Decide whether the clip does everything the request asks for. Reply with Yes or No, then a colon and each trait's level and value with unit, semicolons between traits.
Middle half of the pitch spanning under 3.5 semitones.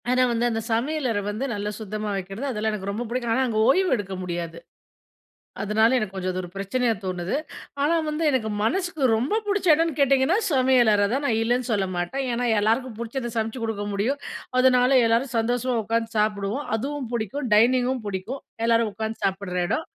No: average, 3.9 semitones